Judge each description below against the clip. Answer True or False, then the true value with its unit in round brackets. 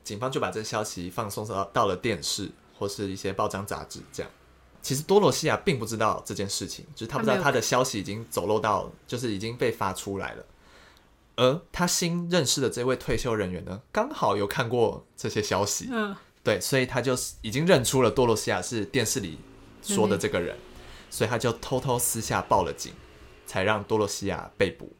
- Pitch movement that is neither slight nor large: True (4.8 semitones)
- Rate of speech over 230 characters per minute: True (300 characters per minute)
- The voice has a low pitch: True (115 Hz)